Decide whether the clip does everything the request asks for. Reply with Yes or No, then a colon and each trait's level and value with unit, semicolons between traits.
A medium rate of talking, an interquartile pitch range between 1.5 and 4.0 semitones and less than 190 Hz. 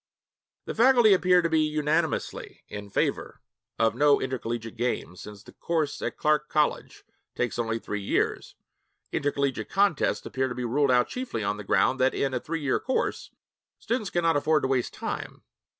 No: average, 170 wpm; average, 5.2 semitones; medium, 140 Hz